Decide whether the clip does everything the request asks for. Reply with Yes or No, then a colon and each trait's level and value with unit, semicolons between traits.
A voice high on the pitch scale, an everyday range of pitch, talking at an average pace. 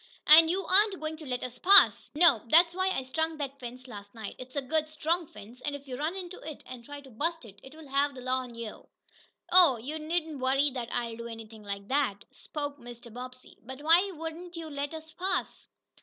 No: very high, 285 Hz; average, 4.6 semitones; fast, 220 wpm